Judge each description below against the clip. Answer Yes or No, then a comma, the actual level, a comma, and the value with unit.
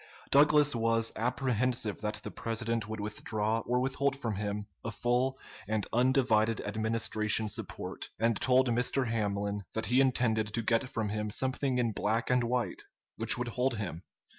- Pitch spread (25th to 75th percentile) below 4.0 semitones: Yes, average, 2.8 semitones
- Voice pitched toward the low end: Yes, low, 115 Hz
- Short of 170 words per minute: Yes, average, 160 wpm